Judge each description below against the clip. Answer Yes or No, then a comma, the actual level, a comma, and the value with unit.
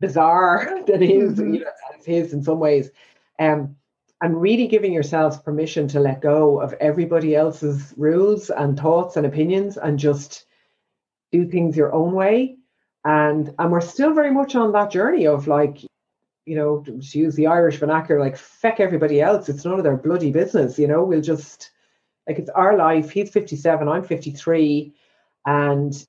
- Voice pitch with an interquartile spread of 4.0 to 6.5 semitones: No, average, 3.1 semitones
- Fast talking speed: No, average, 165 wpm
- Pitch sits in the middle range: Yes, medium, 155 Hz